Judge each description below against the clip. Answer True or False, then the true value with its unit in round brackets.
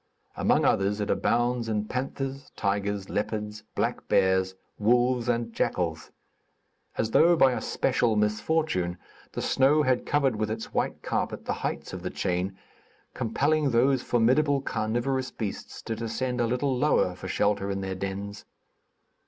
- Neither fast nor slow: True (145 wpm)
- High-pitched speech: False (115 Hz)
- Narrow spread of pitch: False (4.4 semitones)